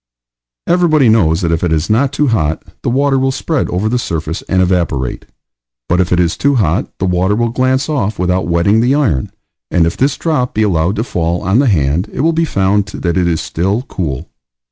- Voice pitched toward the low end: Yes, very low, 95 Hz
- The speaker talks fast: Yes, fast, 215 wpm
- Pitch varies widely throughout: Yes, wide, 7.1 semitones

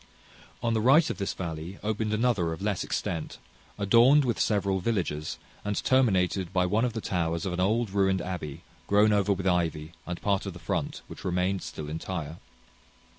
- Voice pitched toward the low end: Yes, very low, 95 Hz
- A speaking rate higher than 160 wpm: Yes, average, 180 wpm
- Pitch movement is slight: No, average, 3.5 semitones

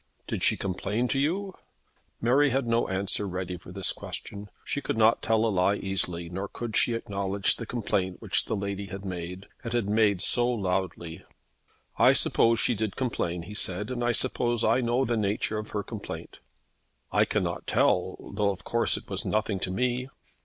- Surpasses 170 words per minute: Yes, average, 190 wpm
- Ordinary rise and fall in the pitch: Yes, average, 3.7 semitones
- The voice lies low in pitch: Yes, low, 105 Hz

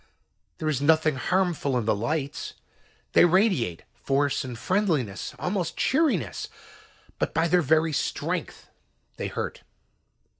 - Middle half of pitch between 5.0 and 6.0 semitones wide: Yes, wide, 5.6 semitones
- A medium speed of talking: No, slow, 120 wpm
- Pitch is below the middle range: No, medium, 155 Hz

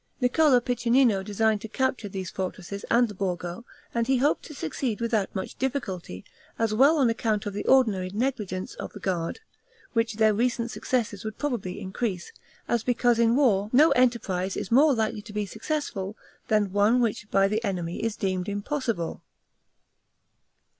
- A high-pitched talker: Yes, high, 220 Hz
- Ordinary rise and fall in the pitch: Yes, average, 4.0 semitones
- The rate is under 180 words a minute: Yes, average, 165 wpm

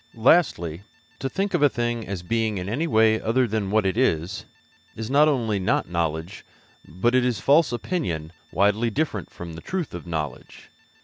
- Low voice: Yes, low, 110 Hz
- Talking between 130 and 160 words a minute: No, average, 180 wpm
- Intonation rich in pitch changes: Yes, wide, 6.4 semitones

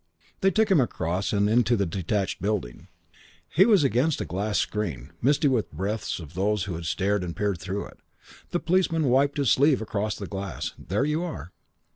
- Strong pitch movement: Yes, wide, 6.8 semitones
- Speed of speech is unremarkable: Yes, average, 190 wpm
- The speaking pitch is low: Yes, low, 105 Hz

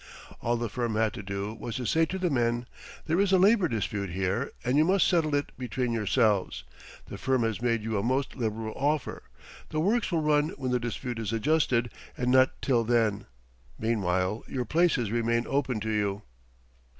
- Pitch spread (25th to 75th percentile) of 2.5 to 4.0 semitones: No, average, 4.7 semitones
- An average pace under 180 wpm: No, average, 190 wpm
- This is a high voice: No, low, 120 Hz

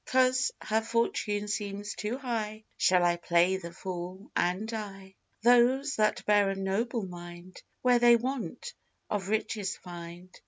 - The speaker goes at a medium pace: Yes, average, 145 wpm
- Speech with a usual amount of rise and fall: Yes, average, 4.0 semitones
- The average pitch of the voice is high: Yes, high, 210 Hz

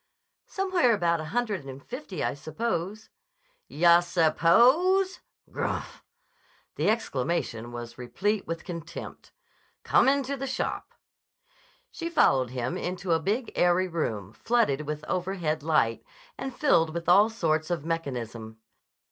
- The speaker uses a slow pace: Yes, slow, 130 wpm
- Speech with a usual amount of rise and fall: No, wide, 6.8 semitones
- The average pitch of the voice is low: No, medium, 170 Hz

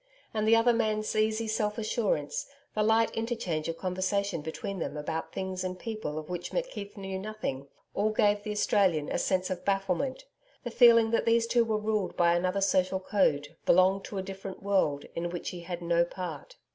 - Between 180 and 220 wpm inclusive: Yes, average, 190 wpm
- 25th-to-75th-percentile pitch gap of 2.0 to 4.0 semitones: Yes, average, 3.5 semitones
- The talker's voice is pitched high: Yes, high, 195 Hz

